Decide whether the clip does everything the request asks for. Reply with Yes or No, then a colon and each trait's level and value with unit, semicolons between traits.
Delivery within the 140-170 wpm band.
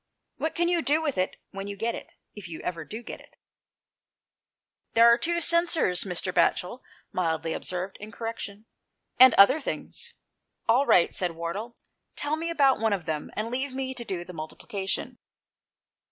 No: average, 180 wpm